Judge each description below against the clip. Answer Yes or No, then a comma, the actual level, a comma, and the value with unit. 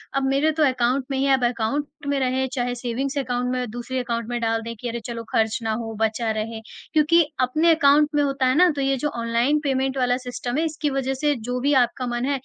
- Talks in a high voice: Yes, very high, 255 Hz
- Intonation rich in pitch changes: No, average, 2.7 semitones